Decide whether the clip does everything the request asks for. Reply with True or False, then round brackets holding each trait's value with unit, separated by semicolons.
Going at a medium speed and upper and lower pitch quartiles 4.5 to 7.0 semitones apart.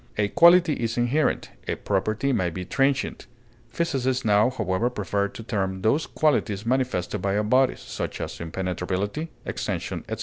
True (155 wpm; 5.4 semitones)